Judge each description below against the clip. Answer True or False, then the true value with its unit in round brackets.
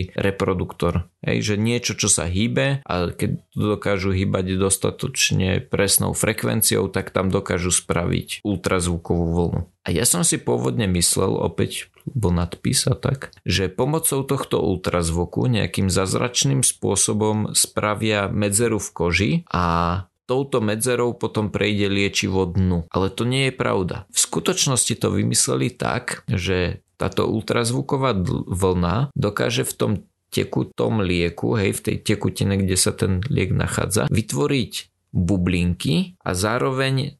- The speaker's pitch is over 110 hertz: False (100 Hz)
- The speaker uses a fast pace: False (125 wpm)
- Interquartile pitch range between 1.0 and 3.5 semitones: False (4.8 semitones)